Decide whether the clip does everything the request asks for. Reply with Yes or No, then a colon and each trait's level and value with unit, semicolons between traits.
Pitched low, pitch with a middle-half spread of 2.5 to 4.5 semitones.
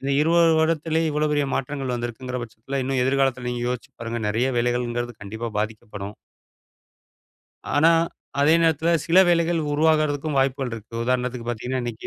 Yes: low, 130 Hz; average, 4.1 semitones